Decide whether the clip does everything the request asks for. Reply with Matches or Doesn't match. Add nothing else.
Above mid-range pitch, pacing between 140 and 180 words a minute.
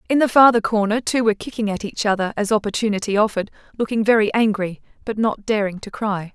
Doesn't match